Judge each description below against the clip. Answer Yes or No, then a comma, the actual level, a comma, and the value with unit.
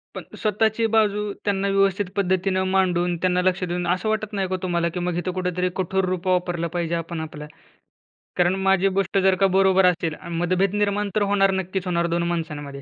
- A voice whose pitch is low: No, medium, 185 Hz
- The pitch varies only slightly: Yes, narrow, 2.1 semitones